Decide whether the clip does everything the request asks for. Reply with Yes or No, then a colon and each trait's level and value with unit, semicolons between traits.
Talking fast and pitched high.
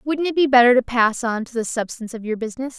Yes: fast, 280 wpm; high, 245 Hz